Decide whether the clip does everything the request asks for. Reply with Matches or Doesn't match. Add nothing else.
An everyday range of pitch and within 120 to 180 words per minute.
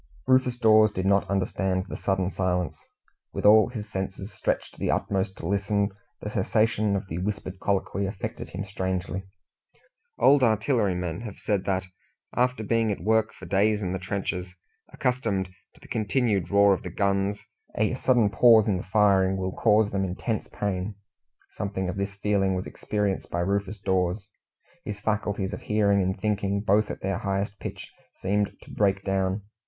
Doesn't match